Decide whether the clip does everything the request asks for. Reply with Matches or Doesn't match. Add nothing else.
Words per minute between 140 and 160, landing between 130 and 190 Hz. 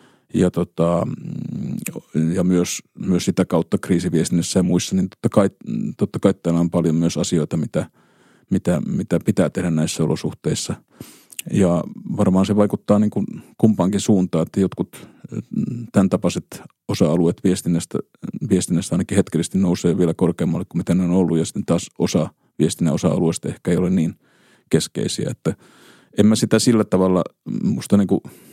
Doesn't match